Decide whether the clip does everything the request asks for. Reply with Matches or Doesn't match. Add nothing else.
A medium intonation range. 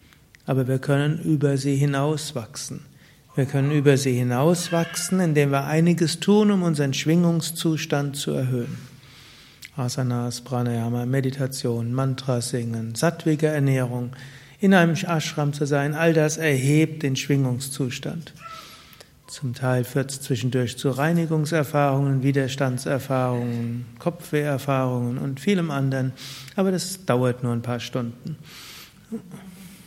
Matches